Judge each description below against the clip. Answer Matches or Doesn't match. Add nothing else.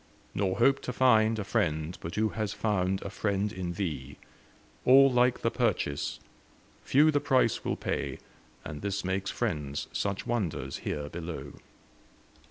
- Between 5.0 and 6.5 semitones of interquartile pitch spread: Matches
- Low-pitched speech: Matches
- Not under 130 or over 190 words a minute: Matches